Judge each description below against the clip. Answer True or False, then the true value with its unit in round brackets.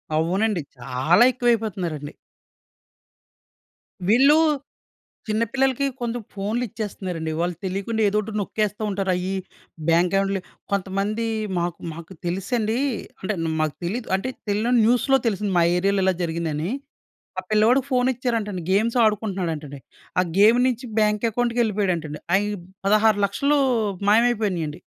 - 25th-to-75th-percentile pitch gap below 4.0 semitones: False (4.3 semitones)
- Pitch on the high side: True (205 Hz)